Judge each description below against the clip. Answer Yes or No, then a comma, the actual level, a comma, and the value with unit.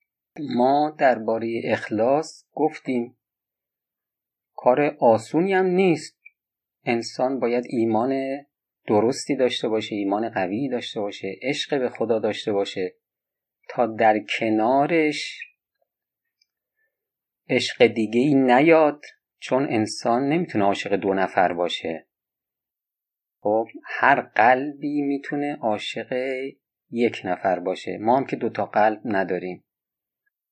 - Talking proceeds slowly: Yes, slow, 100 wpm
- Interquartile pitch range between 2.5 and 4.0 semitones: No, average, 5.1 semitones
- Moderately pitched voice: No, low, 125 Hz